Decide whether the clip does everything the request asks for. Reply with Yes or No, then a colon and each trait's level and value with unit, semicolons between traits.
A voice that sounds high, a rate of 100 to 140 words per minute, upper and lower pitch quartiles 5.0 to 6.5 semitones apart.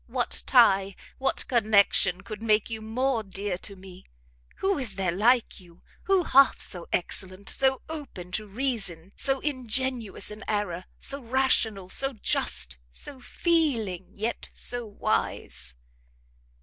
Yes: high, 215 Hz; slow, 135 wpm; wide, 5.4 semitones